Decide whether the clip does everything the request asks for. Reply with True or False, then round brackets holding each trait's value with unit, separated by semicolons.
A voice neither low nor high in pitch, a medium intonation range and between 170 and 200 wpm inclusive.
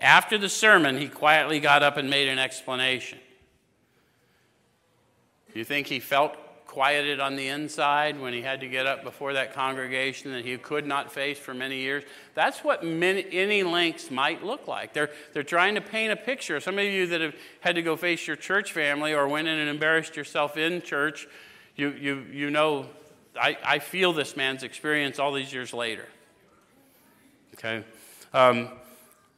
True (145 Hz; 3.1 semitones; 180 wpm)